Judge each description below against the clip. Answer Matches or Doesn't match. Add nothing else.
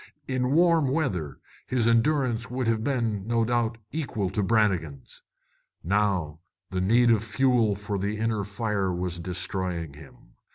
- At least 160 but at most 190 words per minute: Doesn't match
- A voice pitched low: Matches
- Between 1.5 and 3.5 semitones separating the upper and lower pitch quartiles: Doesn't match